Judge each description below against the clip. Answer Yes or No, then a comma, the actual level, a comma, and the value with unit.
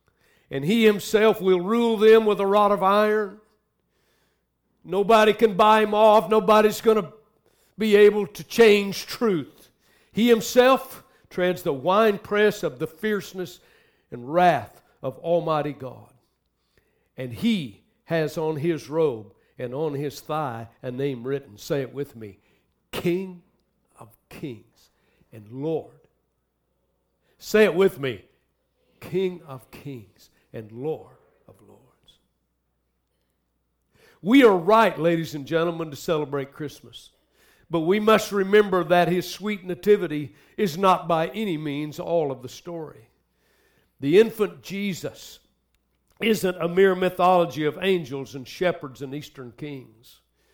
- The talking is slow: Yes, slow, 130 wpm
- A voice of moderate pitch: Yes, medium, 175 Hz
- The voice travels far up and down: Yes, wide, 6.8 semitones